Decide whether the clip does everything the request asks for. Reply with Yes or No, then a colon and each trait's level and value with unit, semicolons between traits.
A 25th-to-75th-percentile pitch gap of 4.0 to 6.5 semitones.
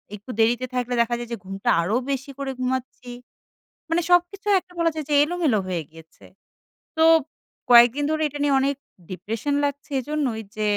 Yes: average, 4.4 semitones